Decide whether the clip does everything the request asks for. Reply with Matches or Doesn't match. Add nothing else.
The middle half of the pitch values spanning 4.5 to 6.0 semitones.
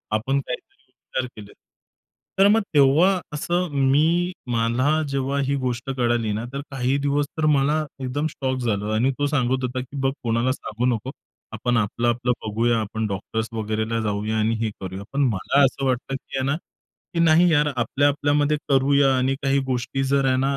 Doesn't match